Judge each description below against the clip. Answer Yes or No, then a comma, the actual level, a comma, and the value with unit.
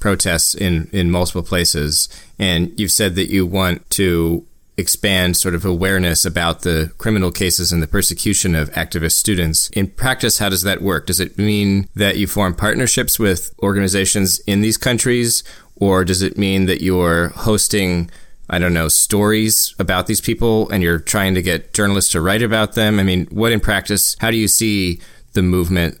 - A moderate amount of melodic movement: Yes, average, 3.0 semitones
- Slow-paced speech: No, average, 180 wpm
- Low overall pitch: Yes, very low, 95 Hz